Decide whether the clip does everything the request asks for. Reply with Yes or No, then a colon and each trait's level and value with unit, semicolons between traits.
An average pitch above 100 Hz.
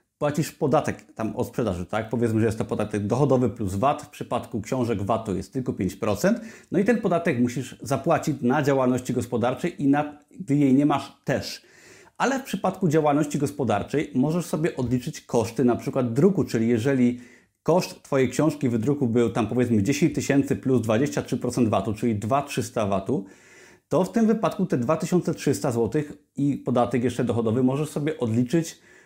Yes: low, 130 Hz